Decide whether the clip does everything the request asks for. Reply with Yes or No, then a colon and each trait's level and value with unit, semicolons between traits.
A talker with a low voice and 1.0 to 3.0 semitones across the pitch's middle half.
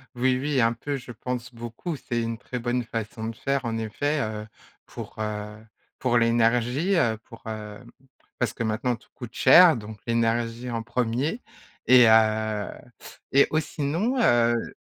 Yes: low, 120 Hz; narrow, 2.4 semitones